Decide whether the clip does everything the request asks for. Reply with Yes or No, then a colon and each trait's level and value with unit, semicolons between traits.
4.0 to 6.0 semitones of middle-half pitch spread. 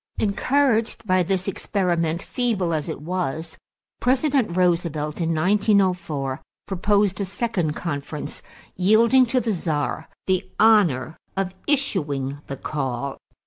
Yes: average, 5.3 semitones